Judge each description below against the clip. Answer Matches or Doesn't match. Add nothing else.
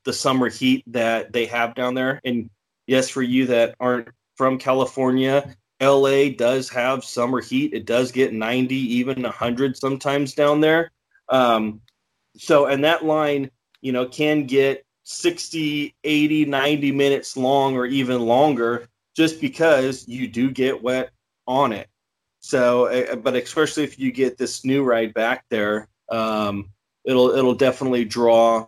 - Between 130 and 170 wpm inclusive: Matches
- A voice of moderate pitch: Doesn't match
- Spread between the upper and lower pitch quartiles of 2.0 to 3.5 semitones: Matches